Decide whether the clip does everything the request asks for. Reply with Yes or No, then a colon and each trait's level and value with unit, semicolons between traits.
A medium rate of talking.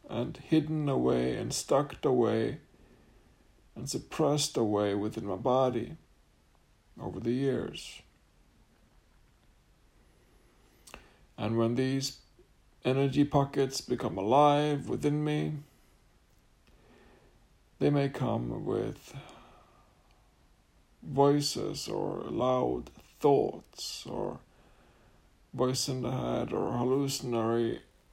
No: slow, 85 wpm